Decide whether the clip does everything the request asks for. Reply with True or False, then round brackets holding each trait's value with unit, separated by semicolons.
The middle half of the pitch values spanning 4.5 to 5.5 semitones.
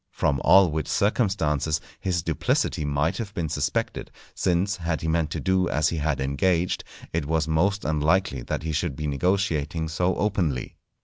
False (3.6 semitones)